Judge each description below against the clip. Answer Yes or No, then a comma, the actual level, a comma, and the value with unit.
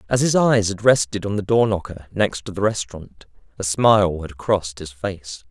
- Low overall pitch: Yes, low, 100 Hz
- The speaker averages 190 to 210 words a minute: Yes, average, 195 wpm